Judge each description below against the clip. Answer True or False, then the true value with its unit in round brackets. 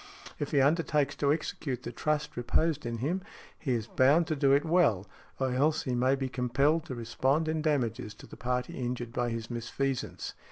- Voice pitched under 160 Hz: True (135 Hz)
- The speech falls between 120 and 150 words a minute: False (195 wpm)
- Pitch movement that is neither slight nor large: True (3.8 semitones)